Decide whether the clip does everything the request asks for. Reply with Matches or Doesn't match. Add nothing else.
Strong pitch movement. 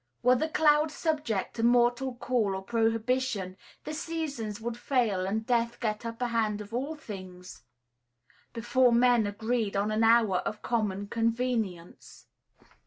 Doesn't match